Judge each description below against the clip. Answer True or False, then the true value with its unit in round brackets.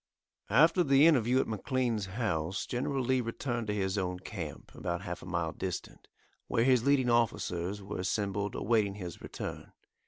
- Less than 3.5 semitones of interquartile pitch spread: False (5.1 semitones)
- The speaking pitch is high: False (105 Hz)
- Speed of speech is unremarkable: True (160 wpm)